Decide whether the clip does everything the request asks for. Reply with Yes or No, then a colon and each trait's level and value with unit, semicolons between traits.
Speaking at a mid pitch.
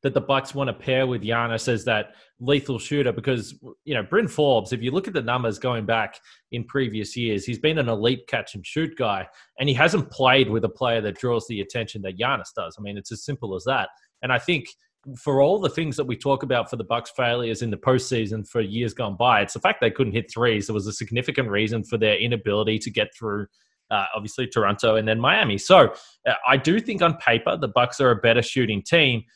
No: low, 120 Hz